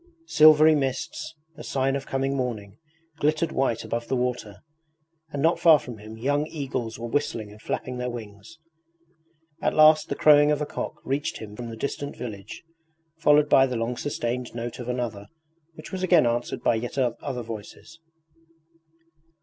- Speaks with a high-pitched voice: No, low, 125 Hz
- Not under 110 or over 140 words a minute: No, average, 165 wpm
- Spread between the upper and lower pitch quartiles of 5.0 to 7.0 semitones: No, average, 4.1 semitones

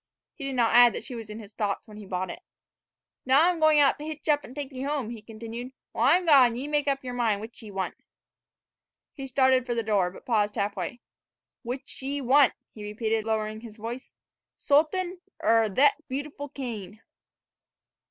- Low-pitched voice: No, high, 245 Hz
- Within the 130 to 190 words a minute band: No, fast, 205 wpm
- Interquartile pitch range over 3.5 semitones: Yes, average, 4.5 semitones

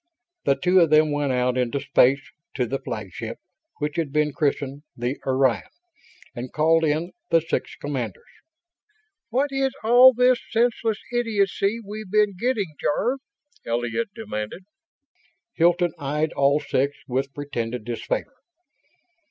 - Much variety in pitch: Yes, wide, 7.6 semitones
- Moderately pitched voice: Yes, medium, 150 Hz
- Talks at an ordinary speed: No, slow, 125 wpm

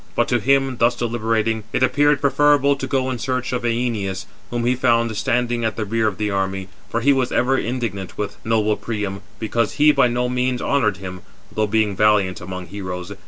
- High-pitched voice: No, low, 115 Hz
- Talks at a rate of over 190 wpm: Yes, average, 200 wpm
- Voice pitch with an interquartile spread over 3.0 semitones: Yes, average, 3.6 semitones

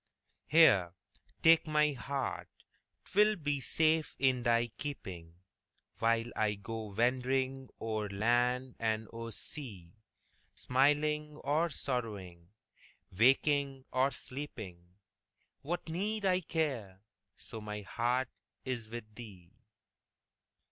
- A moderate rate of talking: No, slow, 100 wpm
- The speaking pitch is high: No, low, 125 Hz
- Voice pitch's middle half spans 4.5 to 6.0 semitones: Yes, average, 5.1 semitones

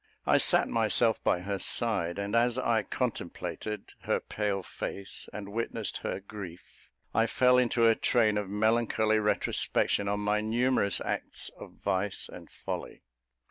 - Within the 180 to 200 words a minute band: No, average, 145 wpm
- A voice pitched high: No, low, 105 Hz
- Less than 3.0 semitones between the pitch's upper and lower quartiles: Yes, narrow, 2.5 semitones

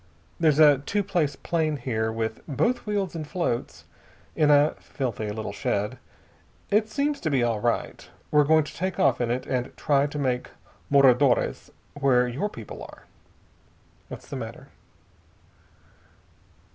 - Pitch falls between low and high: Yes, medium, 145 Hz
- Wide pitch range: No, average, 4.8 semitones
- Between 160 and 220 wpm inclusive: No, average, 145 wpm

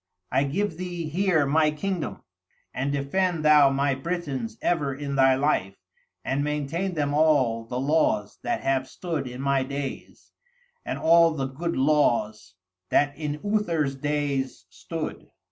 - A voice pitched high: No, medium, 145 Hz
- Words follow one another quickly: No, average, 145 wpm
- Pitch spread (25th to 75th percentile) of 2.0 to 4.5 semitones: Yes, average, 3.2 semitones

